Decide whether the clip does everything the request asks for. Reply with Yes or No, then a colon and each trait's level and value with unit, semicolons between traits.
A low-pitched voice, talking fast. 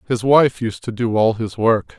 Yes: low, 115 Hz; fast, 240 wpm